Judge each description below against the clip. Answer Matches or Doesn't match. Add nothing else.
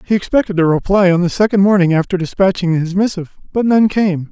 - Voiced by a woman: Doesn't match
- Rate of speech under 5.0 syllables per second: Doesn't match